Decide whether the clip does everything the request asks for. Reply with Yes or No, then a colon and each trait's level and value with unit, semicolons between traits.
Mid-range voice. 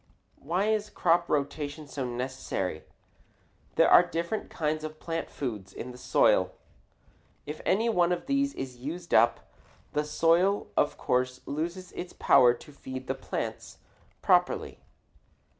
Yes: medium, 150 Hz